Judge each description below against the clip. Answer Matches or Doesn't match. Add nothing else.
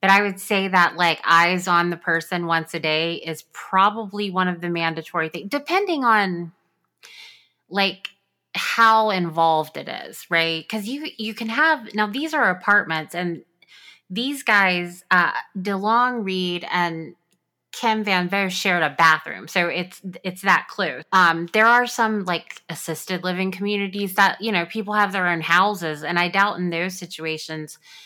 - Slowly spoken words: Doesn't match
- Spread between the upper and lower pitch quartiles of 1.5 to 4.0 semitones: Matches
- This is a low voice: Doesn't match